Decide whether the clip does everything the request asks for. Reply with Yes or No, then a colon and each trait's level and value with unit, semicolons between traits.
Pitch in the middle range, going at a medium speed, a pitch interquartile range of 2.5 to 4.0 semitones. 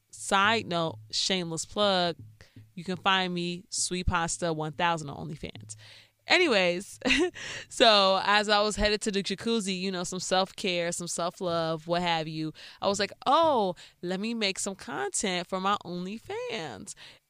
Yes: medium, 180 Hz; average, 155 wpm; average, 3.4 semitones